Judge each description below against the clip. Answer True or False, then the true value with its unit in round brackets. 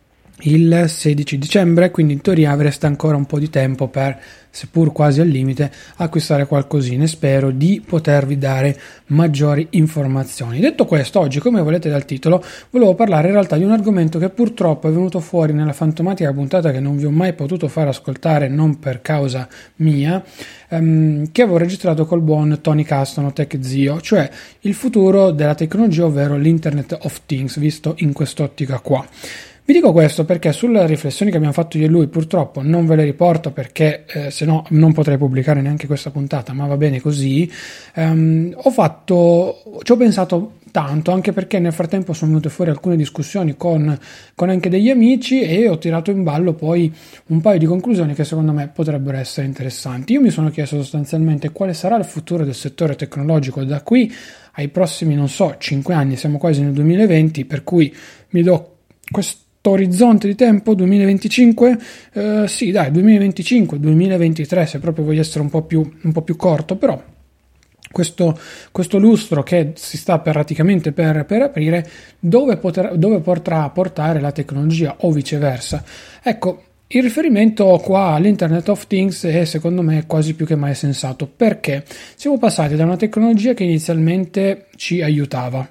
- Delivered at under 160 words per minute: False (170 wpm)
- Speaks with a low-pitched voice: False (160 Hz)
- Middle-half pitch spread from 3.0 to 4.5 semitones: True (3.9 semitones)